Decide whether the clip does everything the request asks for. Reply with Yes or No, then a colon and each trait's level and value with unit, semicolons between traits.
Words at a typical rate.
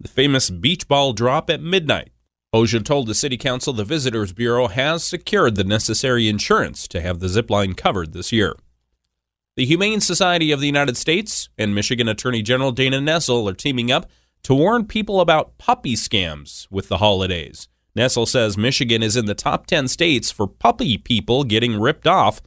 Yes: average, 180 wpm